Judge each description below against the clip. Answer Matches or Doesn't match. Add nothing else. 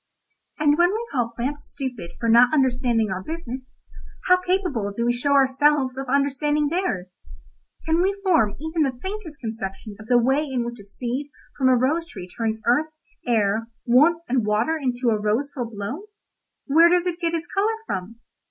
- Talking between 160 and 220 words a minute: Matches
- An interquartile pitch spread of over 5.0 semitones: Matches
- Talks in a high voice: Matches